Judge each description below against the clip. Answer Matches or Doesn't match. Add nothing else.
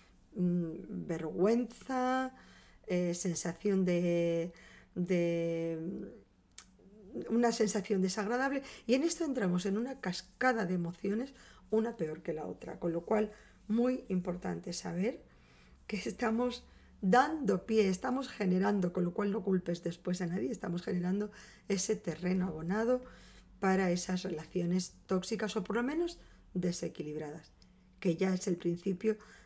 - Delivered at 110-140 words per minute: Matches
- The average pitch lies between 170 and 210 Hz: Matches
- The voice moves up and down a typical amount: Matches